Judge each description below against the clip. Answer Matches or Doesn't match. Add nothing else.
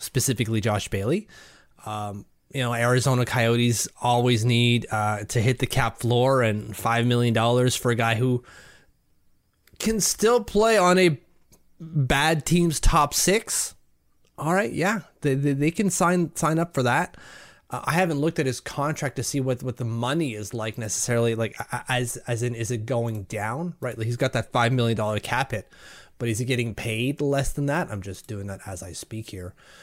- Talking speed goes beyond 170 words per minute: Matches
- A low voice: Matches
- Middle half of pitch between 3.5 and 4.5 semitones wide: Matches